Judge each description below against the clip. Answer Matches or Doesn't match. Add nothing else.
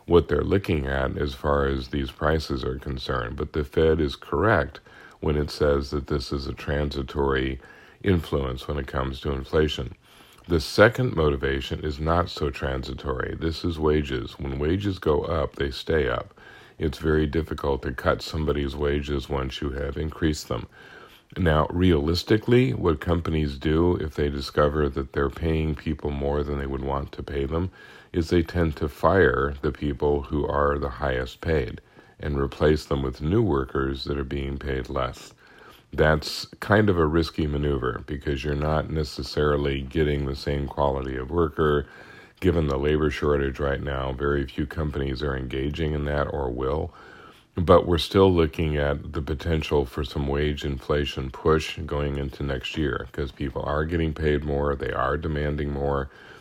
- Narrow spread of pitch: Matches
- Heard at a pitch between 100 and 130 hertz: Doesn't match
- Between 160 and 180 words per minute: Matches